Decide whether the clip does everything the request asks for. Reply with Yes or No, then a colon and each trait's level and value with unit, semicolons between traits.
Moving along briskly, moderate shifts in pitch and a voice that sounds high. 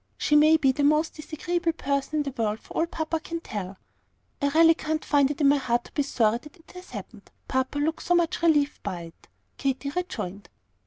Yes: fast, 215 wpm; average, 3.5 semitones; very high, 295 Hz